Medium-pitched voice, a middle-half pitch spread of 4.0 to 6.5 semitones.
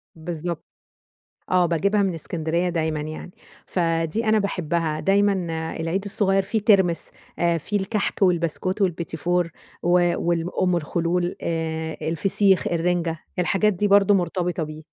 No: medium, 175 Hz; average, 2.7 semitones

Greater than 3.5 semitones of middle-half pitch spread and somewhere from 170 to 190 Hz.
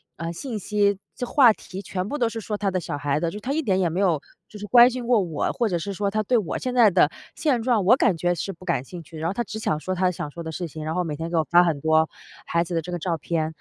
Yes: average, 4.6 semitones; medium, 185 Hz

